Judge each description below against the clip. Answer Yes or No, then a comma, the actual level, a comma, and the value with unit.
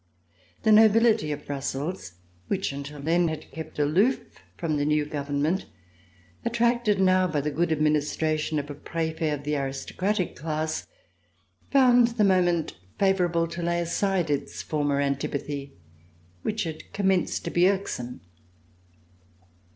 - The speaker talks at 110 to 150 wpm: Yes, slow, 135 wpm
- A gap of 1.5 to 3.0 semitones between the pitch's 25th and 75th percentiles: No, average, 4.5 semitones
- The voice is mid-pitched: Yes, medium, 160 Hz